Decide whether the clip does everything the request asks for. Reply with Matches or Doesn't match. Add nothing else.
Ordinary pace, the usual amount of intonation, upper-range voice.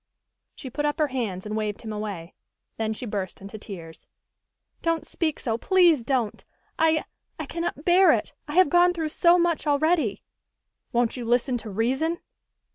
Doesn't match